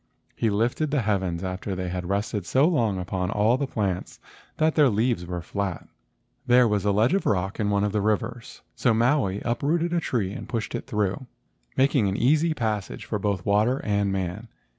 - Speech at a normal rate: Yes, average, 195 wpm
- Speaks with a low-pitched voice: Yes, low, 105 Hz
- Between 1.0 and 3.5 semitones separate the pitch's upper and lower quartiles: No, average, 4.2 semitones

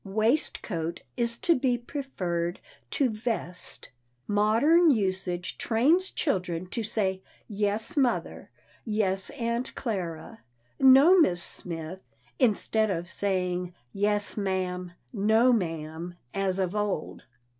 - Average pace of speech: No, slow, 100 wpm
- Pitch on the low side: No, high, 205 Hz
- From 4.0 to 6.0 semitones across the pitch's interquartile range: Yes, average, 4.7 semitones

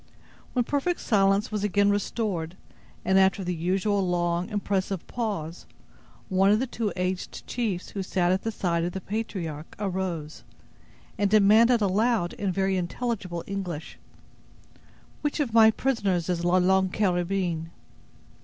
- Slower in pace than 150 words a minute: Yes, average, 140 wpm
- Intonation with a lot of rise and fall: No, average, 3.0 semitones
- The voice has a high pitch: Yes, high, 195 Hz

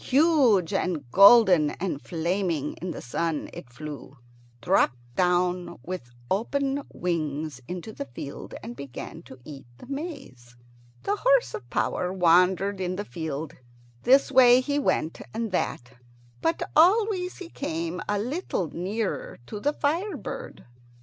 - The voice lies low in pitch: No, medium, 185 Hz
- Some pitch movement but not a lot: No, wide, 8.4 semitones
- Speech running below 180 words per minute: Yes, average, 140 wpm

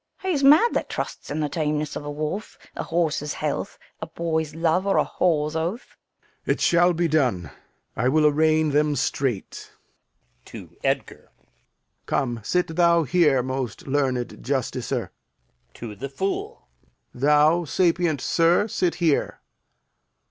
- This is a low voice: No, medium, 155 Hz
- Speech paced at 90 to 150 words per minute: Yes, average, 140 wpm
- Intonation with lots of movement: No, average, 3.7 semitones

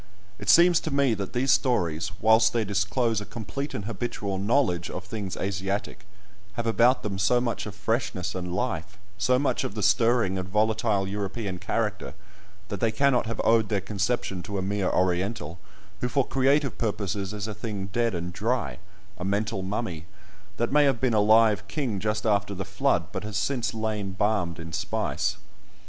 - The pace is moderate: Yes, average, 180 wpm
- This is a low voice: Yes, low, 105 Hz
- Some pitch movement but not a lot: Yes, average, 3.3 semitones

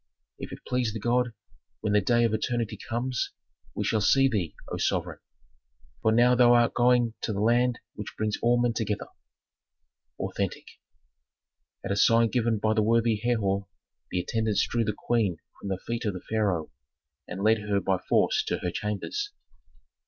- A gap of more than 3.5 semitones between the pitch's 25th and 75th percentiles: No, narrow, 2.4 semitones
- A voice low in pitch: Yes, low, 110 Hz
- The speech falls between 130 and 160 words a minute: No, average, 175 wpm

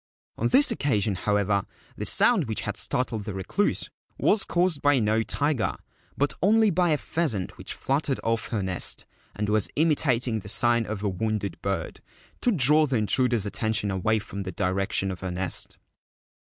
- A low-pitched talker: Yes, low, 110 Hz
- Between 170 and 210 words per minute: Yes, average, 175 wpm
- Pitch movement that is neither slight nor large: No, wide, 6.4 semitones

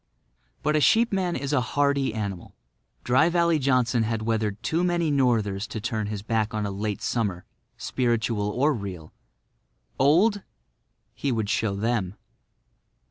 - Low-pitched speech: Yes, low, 115 Hz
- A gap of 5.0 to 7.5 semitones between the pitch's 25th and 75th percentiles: Yes, average, 5.3 semitones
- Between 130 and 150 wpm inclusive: Yes, average, 140 wpm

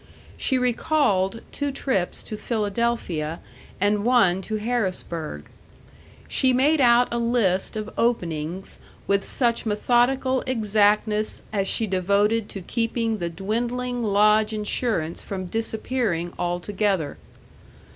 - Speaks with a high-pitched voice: Yes, high, 215 Hz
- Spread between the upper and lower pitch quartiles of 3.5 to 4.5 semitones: Yes, average, 3.9 semitones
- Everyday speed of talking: No, slow, 110 wpm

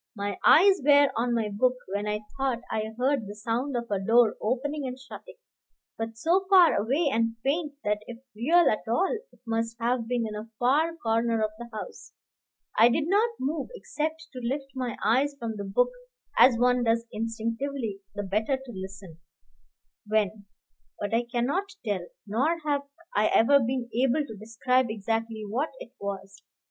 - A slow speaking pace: No, average, 175 wpm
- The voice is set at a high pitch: Yes, high, 235 Hz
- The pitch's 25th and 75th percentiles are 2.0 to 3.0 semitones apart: No, average, 4.3 semitones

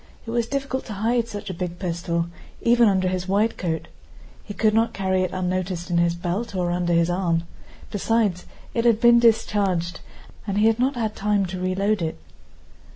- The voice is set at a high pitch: Yes, high, 195 Hz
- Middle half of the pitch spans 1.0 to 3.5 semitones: No, average, 4.1 semitones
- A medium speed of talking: Yes, average, 190 wpm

